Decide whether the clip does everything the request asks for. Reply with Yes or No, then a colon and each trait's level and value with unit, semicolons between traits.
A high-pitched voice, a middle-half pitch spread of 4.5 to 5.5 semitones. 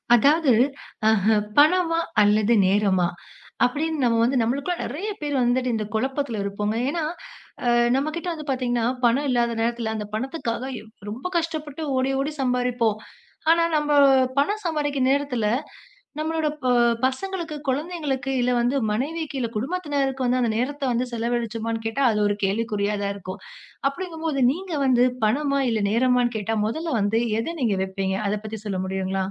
Yes: very high, 250 Hz; average, 5.0 semitones